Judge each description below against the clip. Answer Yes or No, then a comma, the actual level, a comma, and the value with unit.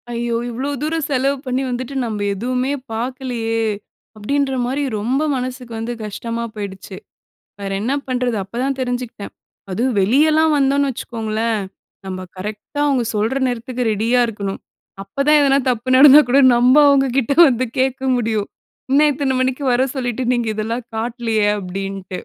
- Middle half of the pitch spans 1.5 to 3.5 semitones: Yes, average, 3.2 semitones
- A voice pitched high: Yes, high, 245 Hz